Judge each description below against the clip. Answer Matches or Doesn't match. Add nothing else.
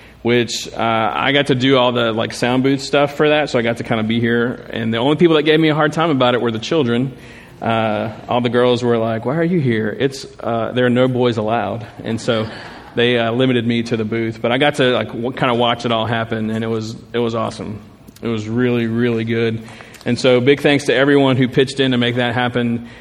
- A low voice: Matches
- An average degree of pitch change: Doesn't match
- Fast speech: Matches